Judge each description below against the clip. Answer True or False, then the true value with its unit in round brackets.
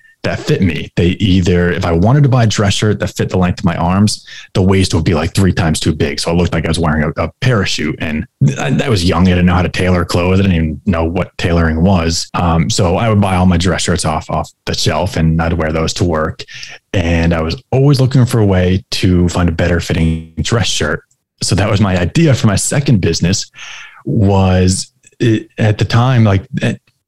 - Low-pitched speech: True (90 Hz)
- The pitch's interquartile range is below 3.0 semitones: False (4.1 semitones)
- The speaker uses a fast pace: True (240 wpm)